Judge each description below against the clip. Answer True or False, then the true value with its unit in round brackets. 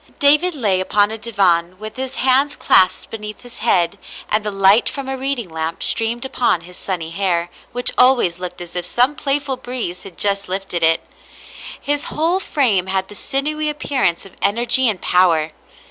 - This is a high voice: True (210 Hz)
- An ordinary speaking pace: True (180 wpm)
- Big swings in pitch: True (6.5 semitones)